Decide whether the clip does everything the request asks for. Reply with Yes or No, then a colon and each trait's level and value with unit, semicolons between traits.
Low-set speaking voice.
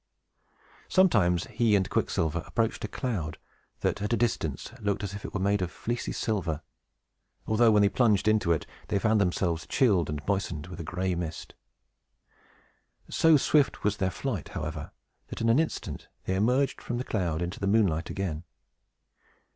Yes: low, 100 Hz